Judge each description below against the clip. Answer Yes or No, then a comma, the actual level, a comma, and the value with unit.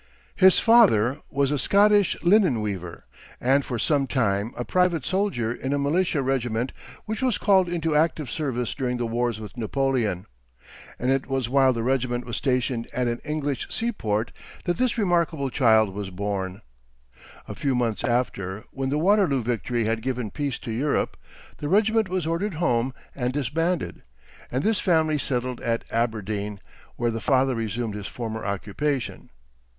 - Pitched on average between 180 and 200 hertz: No, low, 130 Hz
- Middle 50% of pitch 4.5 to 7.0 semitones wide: Yes, wide, 5.4 semitones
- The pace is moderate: Yes, average, 165 wpm